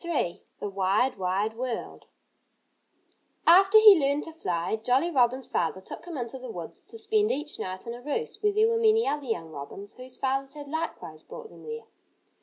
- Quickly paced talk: No, average, 190 wpm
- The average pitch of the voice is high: Yes, very high, 270 Hz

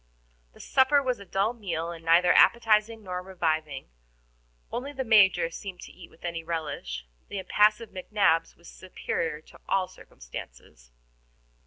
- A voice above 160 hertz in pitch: Yes, medium, 185 Hz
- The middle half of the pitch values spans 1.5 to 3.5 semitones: No, average, 4.4 semitones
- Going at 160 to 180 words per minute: No, average, 145 wpm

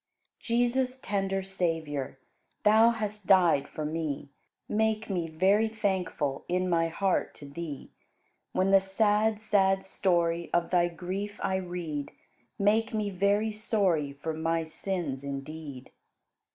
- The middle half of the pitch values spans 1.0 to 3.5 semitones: No, average, 4.2 semitones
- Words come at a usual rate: No, slow, 130 wpm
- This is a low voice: No, medium, 185 Hz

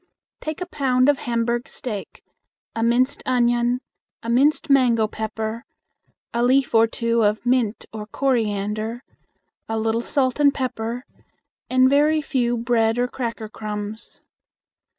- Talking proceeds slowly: Yes, slow, 130 wpm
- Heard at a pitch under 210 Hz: No, high, 240 Hz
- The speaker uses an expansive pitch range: No, narrow, 2.5 semitones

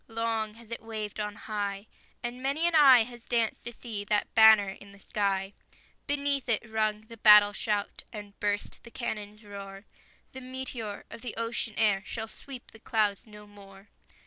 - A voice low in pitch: No, high, 220 Hz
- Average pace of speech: Yes, average, 175 wpm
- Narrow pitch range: Yes, narrow, 2.3 semitones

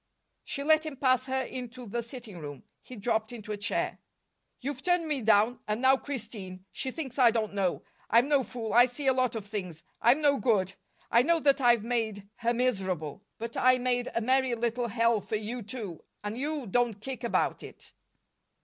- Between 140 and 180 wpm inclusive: No, average, 195 wpm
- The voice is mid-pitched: No, high, 235 Hz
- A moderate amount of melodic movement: Yes, average, 3.4 semitones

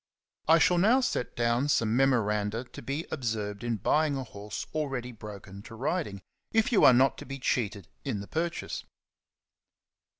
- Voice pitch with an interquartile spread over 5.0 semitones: Yes, wide, 5.6 semitones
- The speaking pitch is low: Yes, low, 120 Hz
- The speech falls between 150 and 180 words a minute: Yes, average, 165 wpm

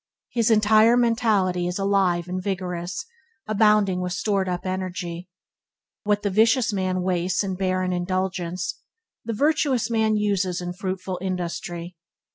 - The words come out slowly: Yes, slow, 130 wpm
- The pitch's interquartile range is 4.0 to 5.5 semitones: No, average, 2.7 semitones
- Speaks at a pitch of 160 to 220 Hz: Yes, high, 190 Hz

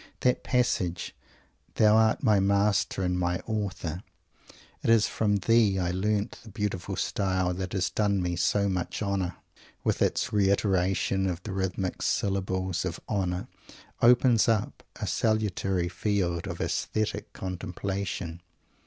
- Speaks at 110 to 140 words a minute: Yes, slow, 135 wpm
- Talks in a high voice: No, very low, 95 Hz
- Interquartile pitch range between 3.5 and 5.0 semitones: No, narrow, 2.6 semitones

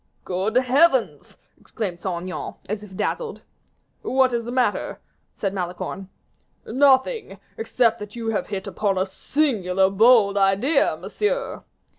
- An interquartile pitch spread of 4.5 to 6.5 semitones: Yes, average, 5.2 semitones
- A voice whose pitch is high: Yes, high, 215 Hz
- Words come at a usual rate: No, slow, 130 wpm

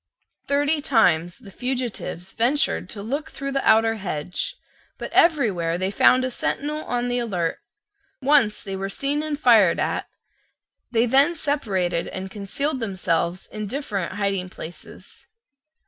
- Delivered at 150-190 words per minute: No, average, 140 wpm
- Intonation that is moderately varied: No, wide, 6.5 semitones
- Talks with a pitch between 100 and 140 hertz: No, high, 225 Hz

